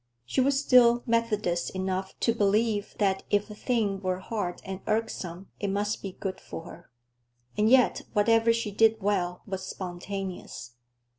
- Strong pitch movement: No, average, 3.2 semitones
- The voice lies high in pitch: Yes, high, 205 Hz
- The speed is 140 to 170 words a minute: Yes, average, 155 wpm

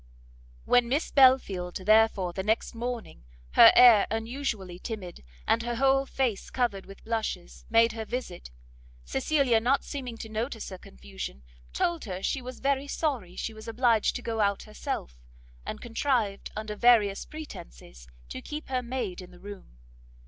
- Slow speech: No, average, 155 wpm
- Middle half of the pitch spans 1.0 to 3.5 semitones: No, average, 4.5 semitones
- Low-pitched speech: No, high, 225 Hz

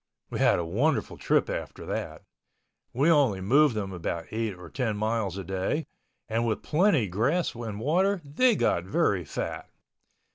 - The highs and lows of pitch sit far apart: Yes, wide, 7.6 semitones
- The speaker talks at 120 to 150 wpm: No, average, 160 wpm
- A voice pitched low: Yes, low, 115 Hz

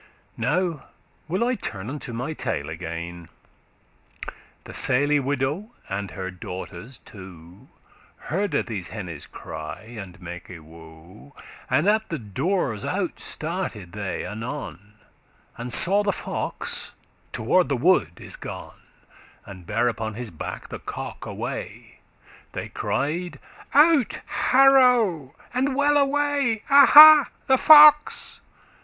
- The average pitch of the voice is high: No, low, 135 Hz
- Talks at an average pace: No, slow, 125 wpm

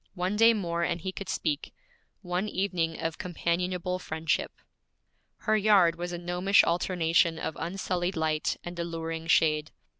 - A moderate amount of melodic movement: No, narrow, 2.1 semitones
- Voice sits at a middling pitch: Yes, medium, 175 Hz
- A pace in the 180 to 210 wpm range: No, average, 145 wpm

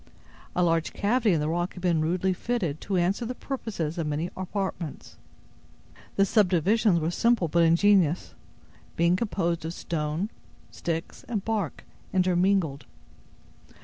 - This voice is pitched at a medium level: Yes, medium, 180 Hz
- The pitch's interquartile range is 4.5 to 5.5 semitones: No, average, 3.5 semitones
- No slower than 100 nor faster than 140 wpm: Yes, slow, 135 wpm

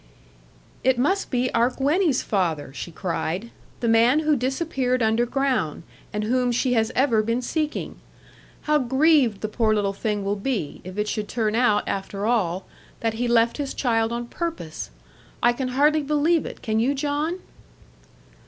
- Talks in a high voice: Yes, high, 240 Hz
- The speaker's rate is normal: Yes, average, 160 wpm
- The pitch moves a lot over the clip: No, average, 4.4 semitones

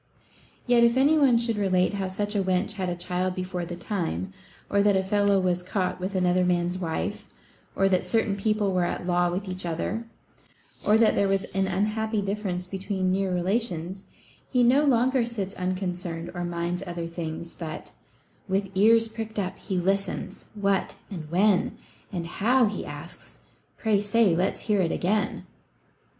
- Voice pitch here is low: No, high, 190 Hz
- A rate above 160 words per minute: Yes, average, 170 wpm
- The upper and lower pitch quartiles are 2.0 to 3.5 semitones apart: Yes, average, 2.8 semitones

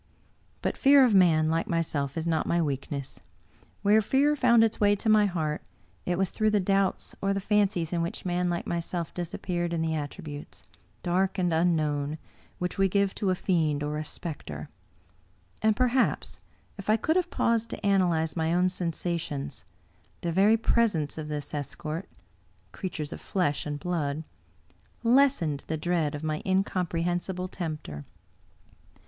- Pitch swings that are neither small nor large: Yes, average, 4.1 semitones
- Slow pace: No, average, 165 wpm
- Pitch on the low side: No, medium, 175 Hz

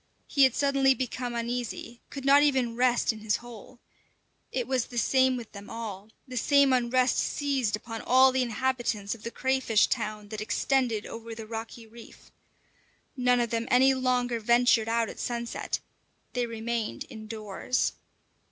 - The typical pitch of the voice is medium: No, high, 240 Hz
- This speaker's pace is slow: No, average, 160 wpm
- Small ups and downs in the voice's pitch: Yes, narrow, 2.3 semitones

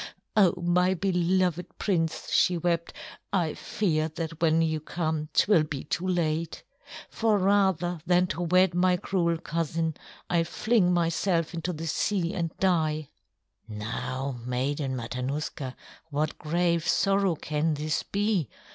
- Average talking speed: No, slow, 130 wpm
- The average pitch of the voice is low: No, medium, 170 Hz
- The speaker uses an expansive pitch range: No, average, 2.7 semitones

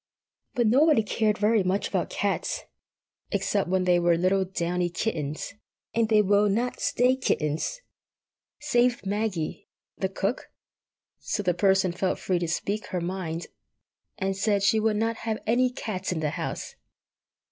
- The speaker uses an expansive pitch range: No, average, 3.7 semitones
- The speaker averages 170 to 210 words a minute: No, average, 145 wpm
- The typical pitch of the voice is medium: No, high, 200 Hz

